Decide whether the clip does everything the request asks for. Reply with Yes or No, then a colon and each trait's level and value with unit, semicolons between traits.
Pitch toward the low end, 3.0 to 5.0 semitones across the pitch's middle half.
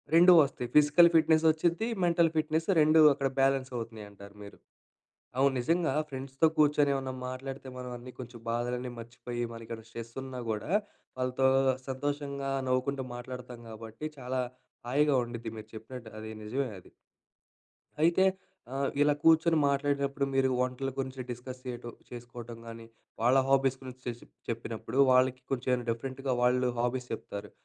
No: low, 130 Hz; narrow, 2.6 semitones